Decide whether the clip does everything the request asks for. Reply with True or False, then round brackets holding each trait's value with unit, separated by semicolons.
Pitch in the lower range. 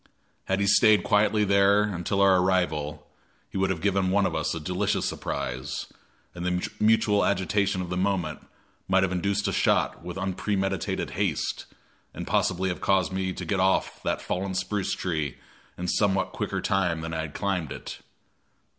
True (95 Hz)